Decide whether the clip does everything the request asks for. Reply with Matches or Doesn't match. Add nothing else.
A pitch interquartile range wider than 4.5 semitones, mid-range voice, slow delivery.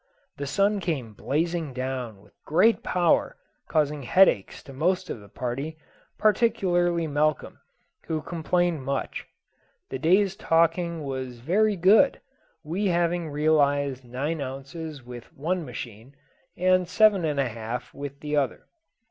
Matches